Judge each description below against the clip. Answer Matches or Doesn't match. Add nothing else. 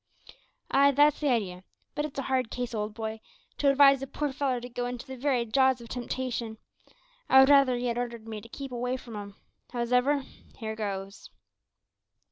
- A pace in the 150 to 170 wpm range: Doesn't match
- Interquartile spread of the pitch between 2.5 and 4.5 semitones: Matches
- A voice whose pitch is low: Doesn't match